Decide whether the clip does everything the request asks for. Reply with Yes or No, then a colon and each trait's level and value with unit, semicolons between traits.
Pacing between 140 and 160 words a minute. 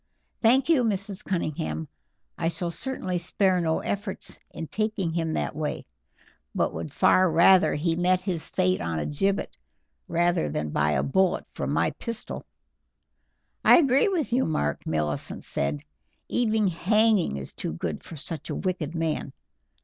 Yes: average, 150 wpm